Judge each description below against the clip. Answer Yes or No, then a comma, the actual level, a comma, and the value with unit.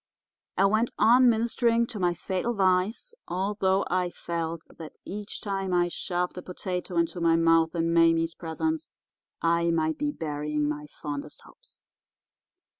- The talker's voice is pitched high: No, medium, 180 Hz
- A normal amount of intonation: Yes, average, 3.8 semitones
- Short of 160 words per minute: Yes, average, 145 wpm